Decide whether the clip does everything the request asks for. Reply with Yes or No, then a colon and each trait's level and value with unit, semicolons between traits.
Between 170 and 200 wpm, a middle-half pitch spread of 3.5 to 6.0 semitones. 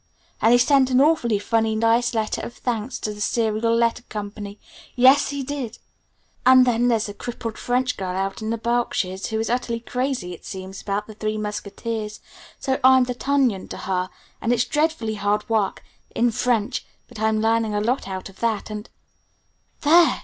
No: average, 185 wpm; average, 2.9 semitones